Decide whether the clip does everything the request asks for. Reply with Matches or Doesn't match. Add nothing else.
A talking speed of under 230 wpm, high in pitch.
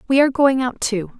Doesn't match